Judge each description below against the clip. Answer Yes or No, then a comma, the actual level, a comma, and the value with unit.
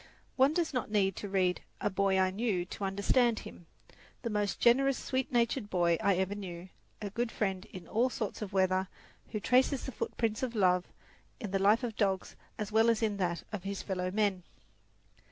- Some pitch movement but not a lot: Yes, average, 3.6 semitones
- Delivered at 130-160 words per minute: No, average, 190 wpm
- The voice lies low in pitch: No, high, 205 Hz